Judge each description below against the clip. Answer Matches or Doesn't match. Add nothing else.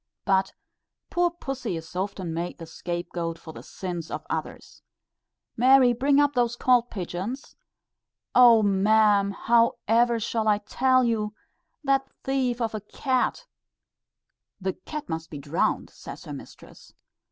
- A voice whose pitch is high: Matches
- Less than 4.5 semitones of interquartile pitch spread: Doesn't match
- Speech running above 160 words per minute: Doesn't match